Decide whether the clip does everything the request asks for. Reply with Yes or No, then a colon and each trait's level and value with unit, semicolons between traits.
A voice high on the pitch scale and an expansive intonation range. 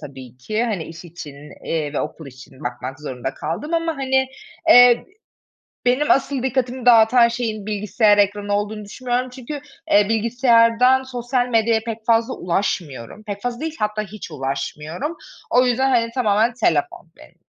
Yes: high, 220 Hz; wide, 6.6 semitones